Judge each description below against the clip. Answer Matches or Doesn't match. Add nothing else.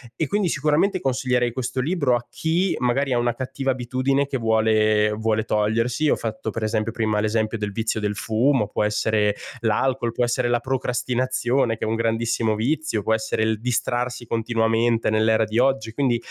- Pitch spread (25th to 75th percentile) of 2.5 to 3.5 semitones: Matches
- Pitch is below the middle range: Matches